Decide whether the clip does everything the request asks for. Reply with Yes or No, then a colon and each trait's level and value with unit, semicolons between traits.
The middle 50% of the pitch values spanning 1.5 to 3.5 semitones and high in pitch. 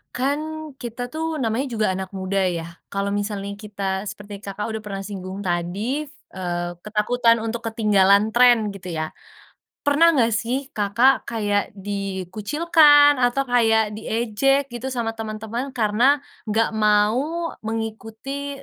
No: average, 4.0 semitones; high, 220 Hz